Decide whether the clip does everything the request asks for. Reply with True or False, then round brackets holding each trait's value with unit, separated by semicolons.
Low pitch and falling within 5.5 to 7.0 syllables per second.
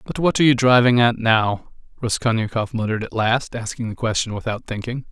True (115 Hz; 5.8 syllables/s)